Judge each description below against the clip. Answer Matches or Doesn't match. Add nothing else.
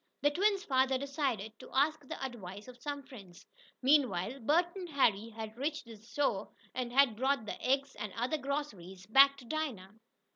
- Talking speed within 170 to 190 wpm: Matches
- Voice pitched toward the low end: Doesn't match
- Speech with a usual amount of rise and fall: Matches